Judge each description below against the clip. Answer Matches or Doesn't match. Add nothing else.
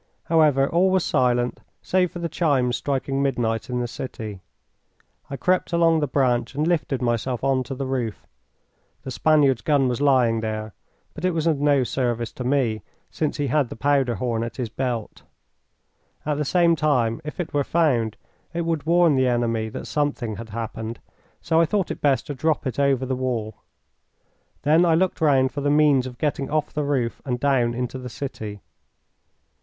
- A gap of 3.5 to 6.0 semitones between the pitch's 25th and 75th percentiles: Matches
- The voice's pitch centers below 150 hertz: Matches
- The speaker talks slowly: Doesn't match